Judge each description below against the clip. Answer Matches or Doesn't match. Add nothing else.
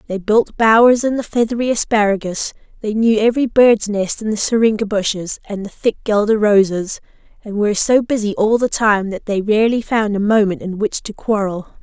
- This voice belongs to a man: Doesn't match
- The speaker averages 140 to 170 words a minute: Doesn't match